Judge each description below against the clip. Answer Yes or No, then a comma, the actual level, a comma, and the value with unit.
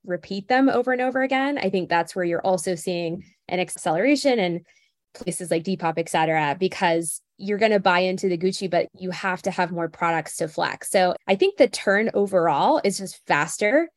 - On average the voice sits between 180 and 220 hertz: Yes, medium, 185 Hz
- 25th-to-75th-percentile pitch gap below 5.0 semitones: Yes, average, 3.7 semitones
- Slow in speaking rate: No, average, 200 wpm